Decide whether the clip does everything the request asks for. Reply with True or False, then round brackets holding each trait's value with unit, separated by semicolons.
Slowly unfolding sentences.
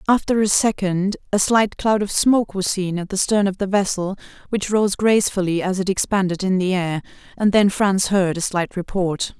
False (205 wpm)